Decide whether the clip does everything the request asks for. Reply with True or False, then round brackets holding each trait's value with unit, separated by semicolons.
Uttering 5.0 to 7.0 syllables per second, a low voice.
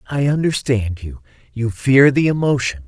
False (4.7 syllables/s; 125 Hz)